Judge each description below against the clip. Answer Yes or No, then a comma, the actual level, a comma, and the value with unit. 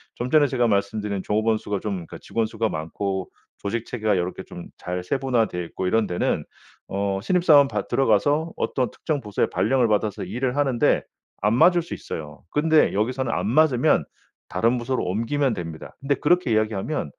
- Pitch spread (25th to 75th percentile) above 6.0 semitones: No, average, 5.2 semitones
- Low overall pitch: Yes, low, 115 Hz